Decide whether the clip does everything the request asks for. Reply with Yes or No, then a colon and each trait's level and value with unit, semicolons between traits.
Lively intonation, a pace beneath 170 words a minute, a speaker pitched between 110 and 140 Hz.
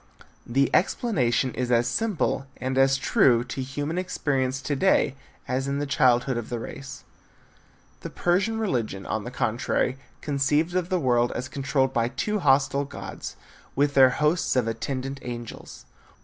No: average, 2.8 semitones; average, 155 wpm; low, 135 Hz